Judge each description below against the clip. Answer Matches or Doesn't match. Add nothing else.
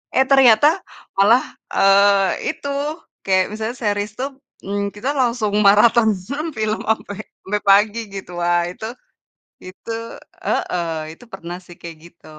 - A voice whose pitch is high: Matches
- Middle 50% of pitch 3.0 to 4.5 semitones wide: Matches